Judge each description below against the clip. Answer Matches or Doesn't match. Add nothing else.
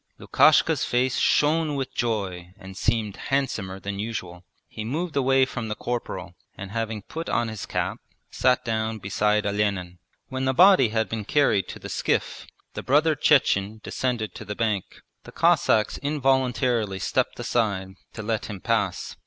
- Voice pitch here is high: Doesn't match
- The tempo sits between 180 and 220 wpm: Doesn't match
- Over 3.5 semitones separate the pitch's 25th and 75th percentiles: Matches